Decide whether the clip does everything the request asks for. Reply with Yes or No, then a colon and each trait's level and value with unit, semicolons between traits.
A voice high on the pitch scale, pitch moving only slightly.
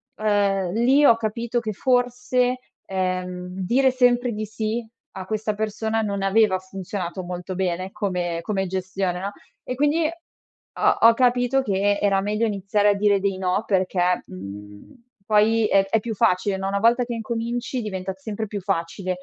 No: high, 205 Hz; average, 3.5 semitones